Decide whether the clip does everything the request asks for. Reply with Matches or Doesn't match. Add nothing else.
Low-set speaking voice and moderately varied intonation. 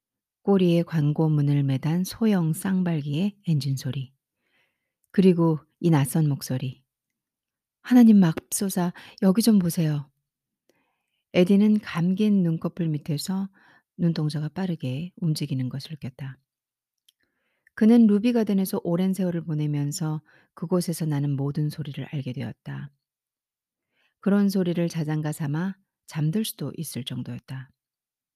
Doesn't match